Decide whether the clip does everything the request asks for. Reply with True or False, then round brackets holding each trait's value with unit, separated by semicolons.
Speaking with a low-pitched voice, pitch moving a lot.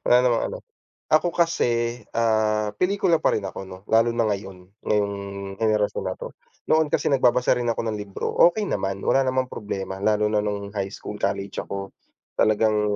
False (110 Hz; 3.4 semitones)